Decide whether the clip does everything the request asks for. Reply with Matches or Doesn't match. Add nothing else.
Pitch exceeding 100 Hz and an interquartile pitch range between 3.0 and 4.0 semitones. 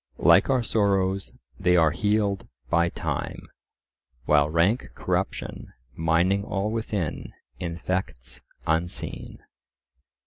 Doesn't match